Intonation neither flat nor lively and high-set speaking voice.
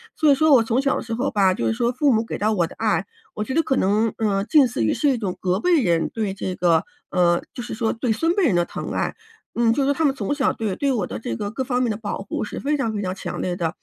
No: wide, 6.0 semitones; high, 220 Hz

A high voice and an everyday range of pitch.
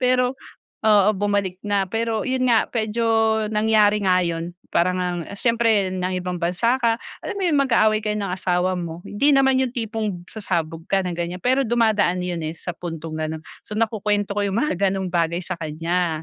Yes: high, 205 Hz; average, 4.2 semitones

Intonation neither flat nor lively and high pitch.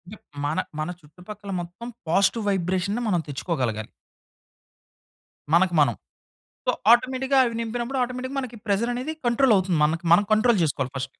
No: wide, 6.1 semitones; high, 200 Hz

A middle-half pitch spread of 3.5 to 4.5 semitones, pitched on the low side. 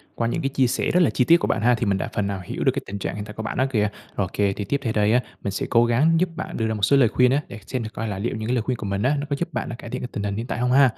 Yes: average, 4.0 semitones; low, 120 Hz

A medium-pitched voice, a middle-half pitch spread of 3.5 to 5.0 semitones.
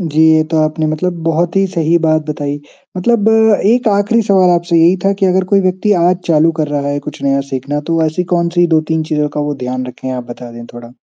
Yes: medium, 165 Hz; average, 3.9 semitones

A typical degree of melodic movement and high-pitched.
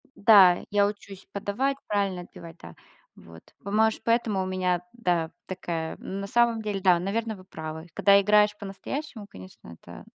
Yes: average, 3.0 semitones; high, 200 Hz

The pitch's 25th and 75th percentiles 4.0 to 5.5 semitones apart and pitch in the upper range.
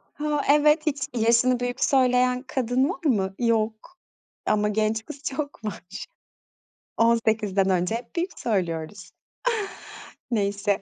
Yes: average, 4.4 semitones; high, 235 Hz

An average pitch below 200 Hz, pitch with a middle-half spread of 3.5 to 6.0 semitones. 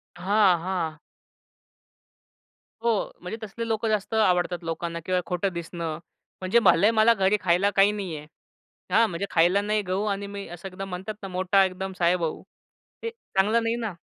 No: high, 190 Hz; average, 3.0 semitones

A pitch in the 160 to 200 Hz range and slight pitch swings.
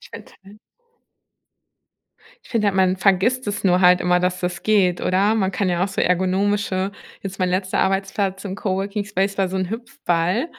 Yes: high, 190 Hz; narrow, 1.8 semitones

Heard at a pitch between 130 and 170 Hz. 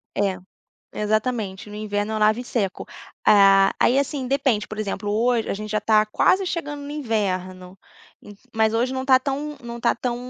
No: high, 220 Hz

